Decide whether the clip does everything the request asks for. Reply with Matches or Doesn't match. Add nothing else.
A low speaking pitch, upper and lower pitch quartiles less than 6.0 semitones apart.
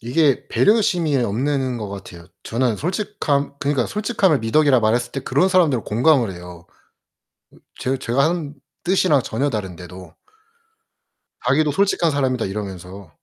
Doesn't match